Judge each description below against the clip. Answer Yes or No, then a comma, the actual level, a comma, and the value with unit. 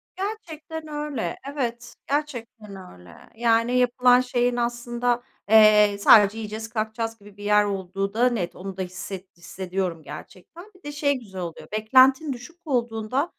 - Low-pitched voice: No, high, 230 Hz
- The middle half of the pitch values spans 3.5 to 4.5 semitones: Yes, average, 4.0 semitones